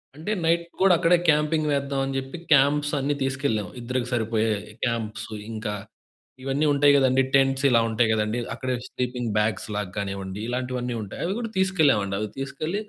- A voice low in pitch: Yes, low, 130 Hz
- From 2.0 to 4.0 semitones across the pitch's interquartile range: No, average, 4.6 semitones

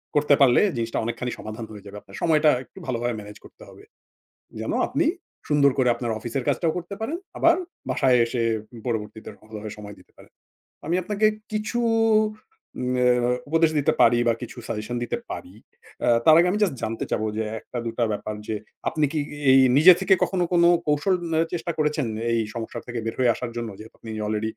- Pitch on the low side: Yes, low, 125 Hz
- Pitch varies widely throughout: Yes, wide, 6.0 semitones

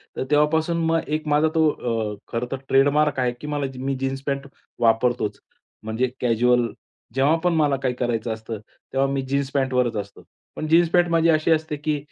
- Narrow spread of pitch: No, average, 3.8 semitones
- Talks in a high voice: No, low, 135 Hz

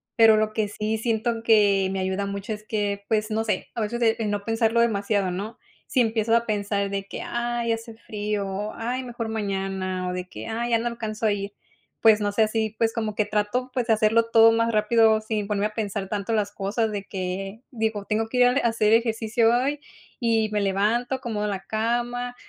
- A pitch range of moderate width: No, narrow, 2.0 semitones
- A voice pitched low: No, high, 220 Hz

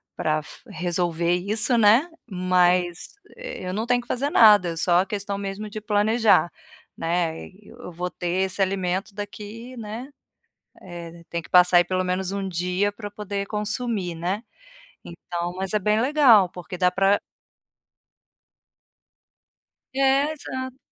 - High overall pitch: Yes, high, 195 Hz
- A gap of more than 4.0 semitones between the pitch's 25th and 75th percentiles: No, average, 3.4 semitones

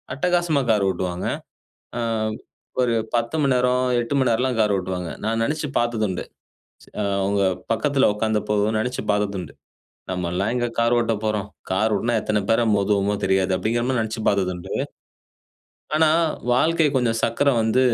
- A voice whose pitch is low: Yes, low, 110 Hz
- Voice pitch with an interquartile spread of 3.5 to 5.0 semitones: Yes, average, 3.8 semitones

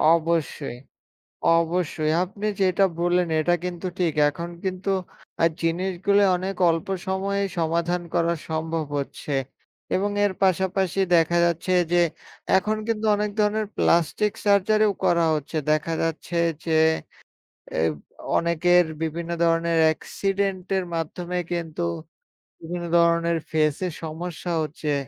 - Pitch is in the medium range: Yes, medium, 175 Hz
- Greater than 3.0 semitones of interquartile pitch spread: No, narrow, 2.5 semitones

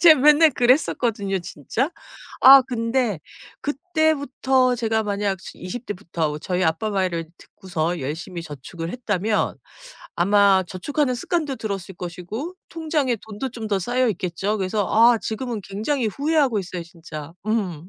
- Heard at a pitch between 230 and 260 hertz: No, high, 215 Hz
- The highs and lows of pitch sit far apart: Yes, wide, 6.0 semitones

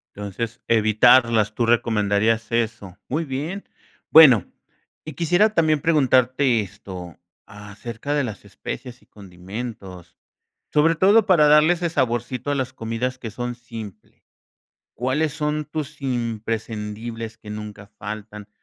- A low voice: Yes, low, 120 Hz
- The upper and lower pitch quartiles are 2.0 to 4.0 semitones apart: No, average, 5.1 semitones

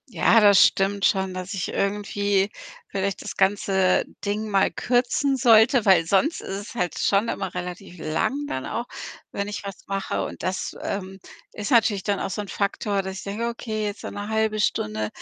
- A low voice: No, high, 200 Hz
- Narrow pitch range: Yes, narrow, 2.2 semitones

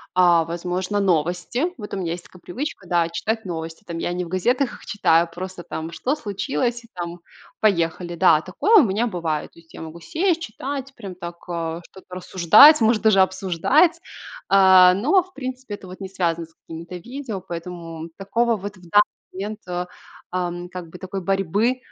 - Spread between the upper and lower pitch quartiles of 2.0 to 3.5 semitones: No, average, 4.2 semitones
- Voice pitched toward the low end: No, medium, 185 Hz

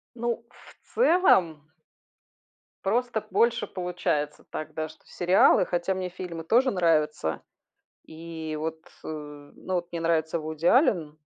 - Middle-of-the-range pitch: Yes, medium, 170 Hz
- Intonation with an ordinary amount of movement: Yes, average, 3.4 semitones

